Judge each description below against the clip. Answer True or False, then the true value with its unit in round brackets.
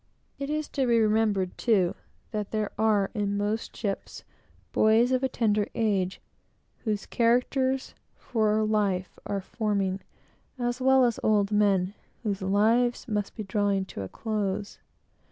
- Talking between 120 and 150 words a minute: True (140 wpm)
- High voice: True (215 Hz)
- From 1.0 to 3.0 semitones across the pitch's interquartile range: True (2.7 semitones)